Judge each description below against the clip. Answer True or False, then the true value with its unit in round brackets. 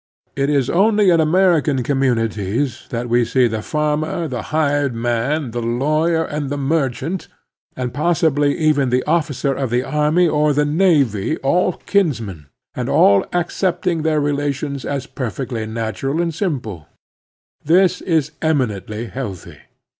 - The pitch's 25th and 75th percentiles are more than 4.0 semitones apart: True (4.7 semitones)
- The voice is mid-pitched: True (145 Hz)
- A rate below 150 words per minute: True (140 wpm)